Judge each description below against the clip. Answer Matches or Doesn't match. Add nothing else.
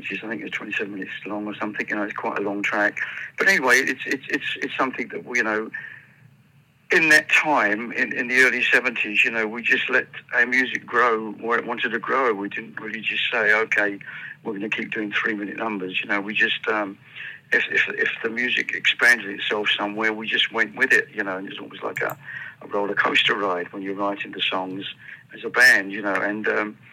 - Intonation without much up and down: Matches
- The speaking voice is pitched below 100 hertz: Doesn't match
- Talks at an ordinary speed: Doesn't match